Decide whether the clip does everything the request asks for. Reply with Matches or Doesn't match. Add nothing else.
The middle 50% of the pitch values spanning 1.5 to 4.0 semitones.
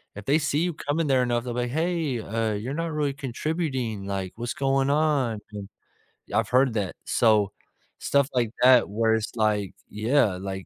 Doesn't match